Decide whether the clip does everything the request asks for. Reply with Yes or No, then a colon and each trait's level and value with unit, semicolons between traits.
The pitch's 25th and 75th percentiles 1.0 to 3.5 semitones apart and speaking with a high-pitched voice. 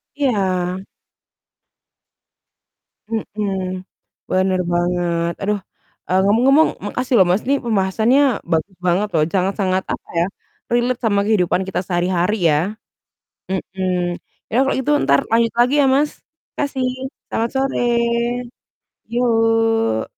No: average, 4.5 semitones; high, 200 Hz